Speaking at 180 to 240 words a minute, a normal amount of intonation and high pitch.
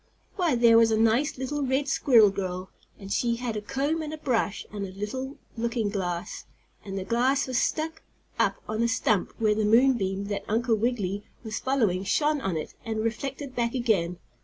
Yes: average, 190 wpm; average, 4.3 semitones; high, 230 Hz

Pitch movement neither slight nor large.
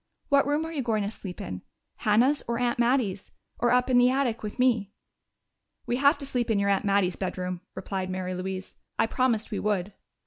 Yes: average, 4.6 semitones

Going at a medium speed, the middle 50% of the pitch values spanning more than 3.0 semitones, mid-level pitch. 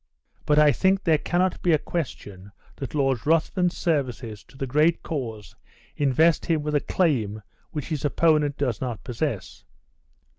Yes: average, 155 wpm; average, 4.6 semitones; medium, 145 Hz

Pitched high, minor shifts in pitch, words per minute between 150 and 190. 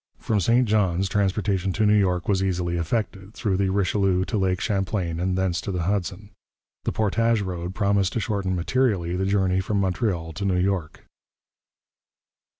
No: very low, 95 Hz; narrow, 2.2 semitones; average, 165 wpm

